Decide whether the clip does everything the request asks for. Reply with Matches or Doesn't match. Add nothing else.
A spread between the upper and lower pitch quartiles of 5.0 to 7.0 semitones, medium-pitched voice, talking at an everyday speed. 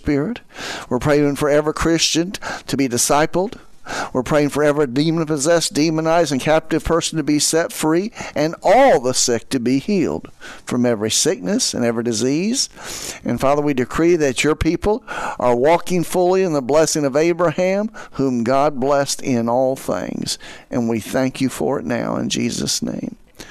Doesn't match